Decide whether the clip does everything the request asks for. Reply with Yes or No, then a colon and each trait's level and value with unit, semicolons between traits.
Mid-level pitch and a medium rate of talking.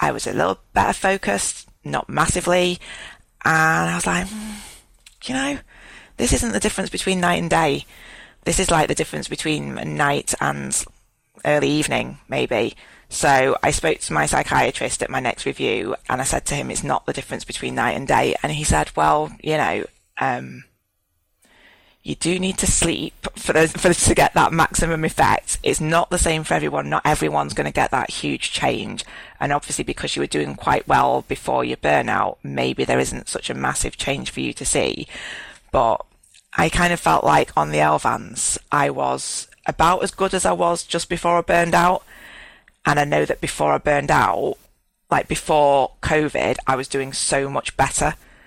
Yes: medium, 155 Hz; average, 190 wpm